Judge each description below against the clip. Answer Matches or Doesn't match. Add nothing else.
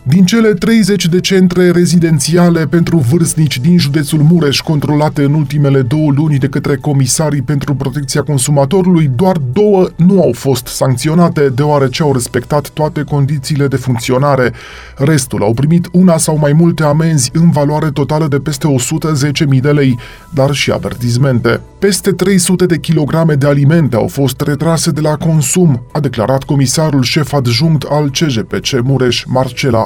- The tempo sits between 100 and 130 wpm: Doesn't match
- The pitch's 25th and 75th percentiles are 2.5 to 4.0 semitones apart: Matches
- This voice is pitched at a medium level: Matches